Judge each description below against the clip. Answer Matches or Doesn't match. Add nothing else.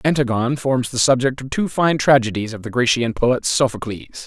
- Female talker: Doesn't match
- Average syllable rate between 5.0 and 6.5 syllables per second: Matches